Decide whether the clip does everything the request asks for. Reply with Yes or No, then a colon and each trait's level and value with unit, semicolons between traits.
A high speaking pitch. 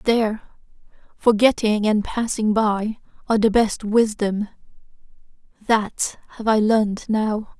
Yes: high, 215 Hz